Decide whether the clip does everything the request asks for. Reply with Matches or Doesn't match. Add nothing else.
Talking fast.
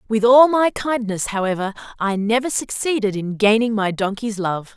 Doesn't match